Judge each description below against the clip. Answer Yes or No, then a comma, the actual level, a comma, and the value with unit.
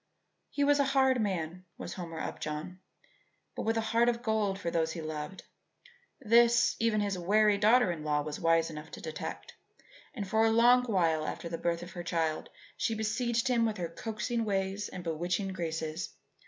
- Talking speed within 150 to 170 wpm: No, average, 185 wpm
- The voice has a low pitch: No, high, 195 Hz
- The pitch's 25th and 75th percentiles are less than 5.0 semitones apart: No, wide, 5.4 semitones